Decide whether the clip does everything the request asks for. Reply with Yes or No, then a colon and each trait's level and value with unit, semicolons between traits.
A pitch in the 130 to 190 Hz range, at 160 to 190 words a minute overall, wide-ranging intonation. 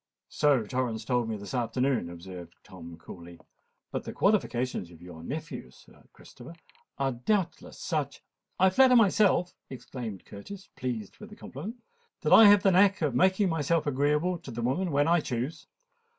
Yes: low, 135 Hz; average, 165 wpm; wide, 8.3 semitones